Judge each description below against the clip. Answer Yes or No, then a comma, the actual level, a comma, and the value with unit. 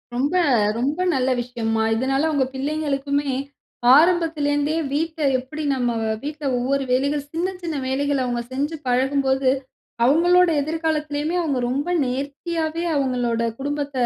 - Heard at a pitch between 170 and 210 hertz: No, very high, 285 Hz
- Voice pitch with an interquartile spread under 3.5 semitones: Yes, average, 2.9 semitones